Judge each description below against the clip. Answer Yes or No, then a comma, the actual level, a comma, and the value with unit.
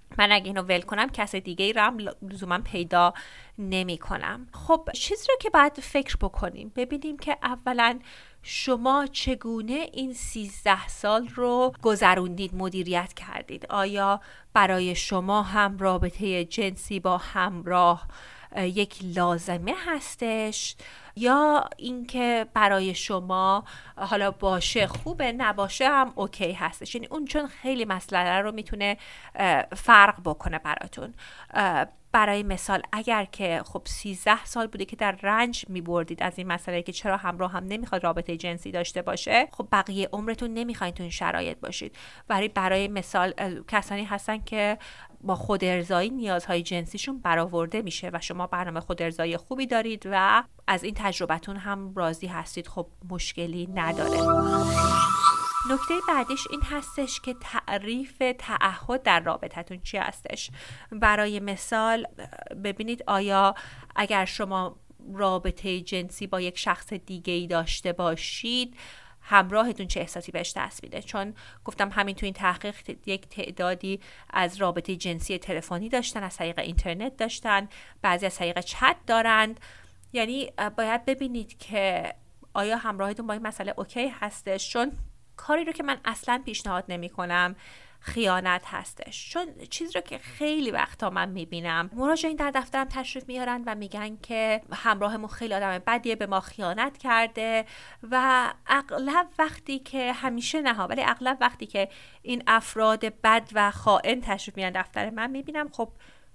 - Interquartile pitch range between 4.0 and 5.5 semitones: Yes, average, 4.4 semitones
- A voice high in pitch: Yes, high, 205 Hz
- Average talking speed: Yes, average, 140 wpm